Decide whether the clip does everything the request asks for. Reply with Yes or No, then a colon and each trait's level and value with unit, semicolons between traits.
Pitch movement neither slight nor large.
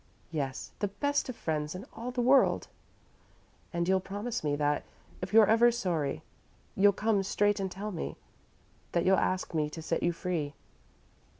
Yes: average, 4.7 semitones